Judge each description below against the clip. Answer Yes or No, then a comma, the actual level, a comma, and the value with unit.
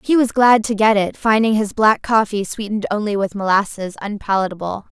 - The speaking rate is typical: Yes, average, 180 wpm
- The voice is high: Yes, high, 210 Hz